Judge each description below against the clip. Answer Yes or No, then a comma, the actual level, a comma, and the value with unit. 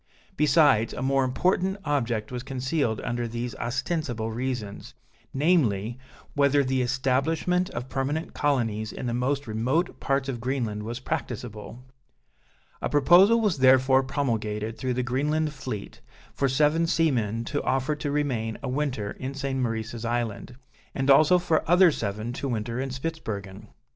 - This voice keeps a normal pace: Yes, average, 145 wpm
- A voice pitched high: No, low, 130 Hz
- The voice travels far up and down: No, average, 3.9 semitones